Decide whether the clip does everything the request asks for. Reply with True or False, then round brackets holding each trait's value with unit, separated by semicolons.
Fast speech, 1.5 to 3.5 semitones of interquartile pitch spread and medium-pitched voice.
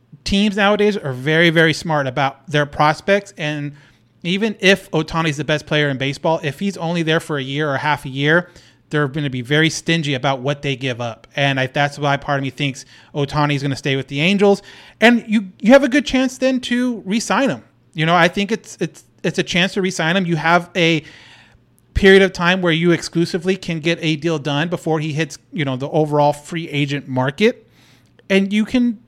False (225 wpm; 5.0 semitones; 160 Hz)